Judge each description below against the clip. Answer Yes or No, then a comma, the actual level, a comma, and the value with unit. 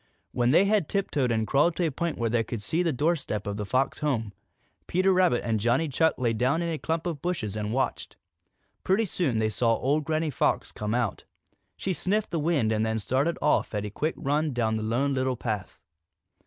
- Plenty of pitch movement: Yes, wide, 6.5 semitones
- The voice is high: No, low, 135 Hz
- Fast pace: Yes, fast, 220 wpm